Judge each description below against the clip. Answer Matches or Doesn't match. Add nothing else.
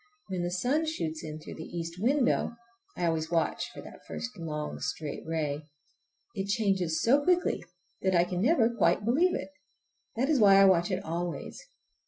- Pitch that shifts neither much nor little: Doesn't match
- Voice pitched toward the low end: Doesn't match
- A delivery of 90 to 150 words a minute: Doesn't match